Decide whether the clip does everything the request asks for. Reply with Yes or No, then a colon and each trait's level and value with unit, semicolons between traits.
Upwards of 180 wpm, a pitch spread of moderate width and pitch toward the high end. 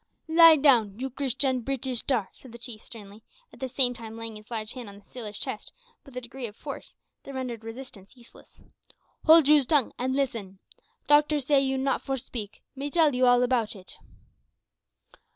Yes: average, 190 wpm; average, 3.2 semitones; very high, 250 Hz